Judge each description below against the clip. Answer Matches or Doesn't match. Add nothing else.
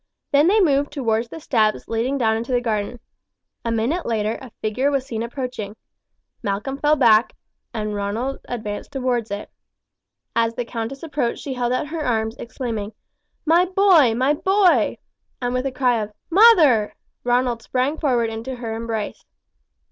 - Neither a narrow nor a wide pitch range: Matches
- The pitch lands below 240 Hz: Doesn't match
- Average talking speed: Matches